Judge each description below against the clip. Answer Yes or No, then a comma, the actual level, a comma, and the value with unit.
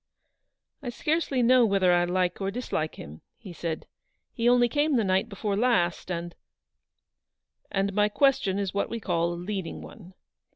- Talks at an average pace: Yes, average, 180 wpm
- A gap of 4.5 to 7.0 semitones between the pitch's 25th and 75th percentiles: Yes, average, 5.2 semitones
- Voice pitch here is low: No, high, 200 Hz